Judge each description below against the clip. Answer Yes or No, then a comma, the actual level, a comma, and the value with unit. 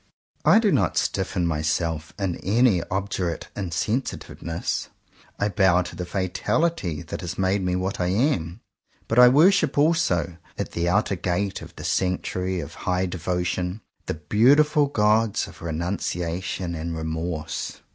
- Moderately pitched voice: No, very low, 90 Hz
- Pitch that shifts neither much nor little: Yes, average, 3.7 semitones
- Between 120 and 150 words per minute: Yes, average, 145 wpm